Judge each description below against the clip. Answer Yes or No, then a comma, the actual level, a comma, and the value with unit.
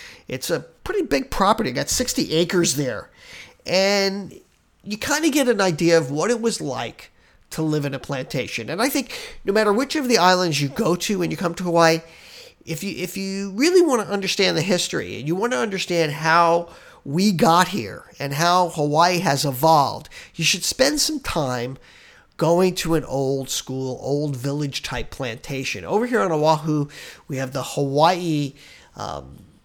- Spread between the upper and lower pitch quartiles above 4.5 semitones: Yes, average, 5.2 semitones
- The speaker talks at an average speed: Yes, average, 185 wpm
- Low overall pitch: No, medium, 170 Hz